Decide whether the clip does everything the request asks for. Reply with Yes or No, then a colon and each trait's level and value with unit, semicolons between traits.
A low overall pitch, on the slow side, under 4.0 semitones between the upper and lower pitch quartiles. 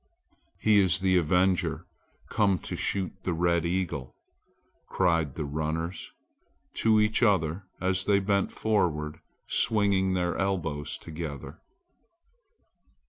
Yes: very low, 90 Hz; slow, 110 wpm; average, 3.4 semitones